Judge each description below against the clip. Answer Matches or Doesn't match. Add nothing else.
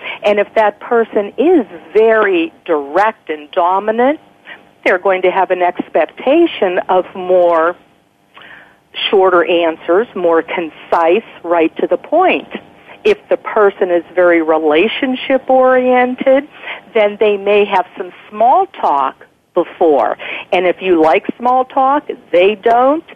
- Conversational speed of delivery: Doesn't match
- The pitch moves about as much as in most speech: Doesn't match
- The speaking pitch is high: Matches